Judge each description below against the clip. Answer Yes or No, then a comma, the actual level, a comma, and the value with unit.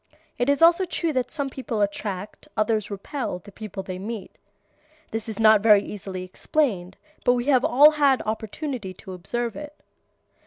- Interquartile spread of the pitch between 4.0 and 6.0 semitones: Yes, wide, 5.4 semitones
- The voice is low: No, high, 225 Hz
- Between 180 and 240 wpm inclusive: No, average, 165 wpm